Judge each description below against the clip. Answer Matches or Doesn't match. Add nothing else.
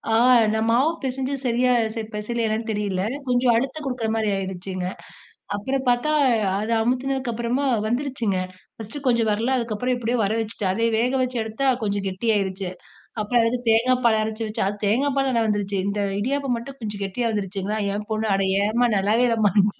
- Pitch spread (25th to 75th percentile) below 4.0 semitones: Matches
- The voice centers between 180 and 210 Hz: Doesn't match